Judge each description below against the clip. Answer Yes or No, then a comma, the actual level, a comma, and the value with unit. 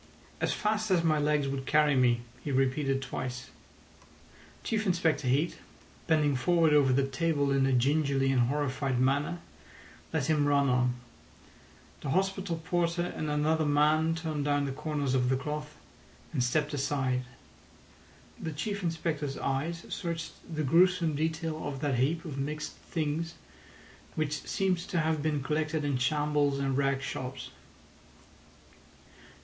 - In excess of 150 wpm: No, average, 145 wpm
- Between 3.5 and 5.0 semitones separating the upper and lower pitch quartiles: No, average, 2.9 semitones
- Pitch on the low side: No, medium, 150 Hz